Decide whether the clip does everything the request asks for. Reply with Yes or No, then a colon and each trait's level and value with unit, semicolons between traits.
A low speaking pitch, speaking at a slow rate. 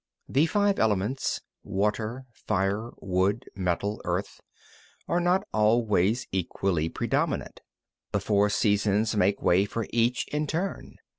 Yes: low, 105 Hz; slow, 130 wpm